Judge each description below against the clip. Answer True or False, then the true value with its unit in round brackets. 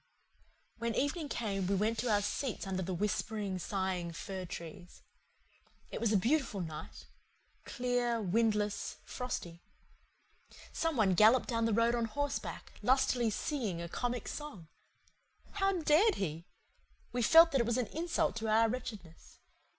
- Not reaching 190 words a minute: True (145 wpm)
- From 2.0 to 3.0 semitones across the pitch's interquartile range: False (4.7 semitones)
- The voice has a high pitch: True (225 Hz)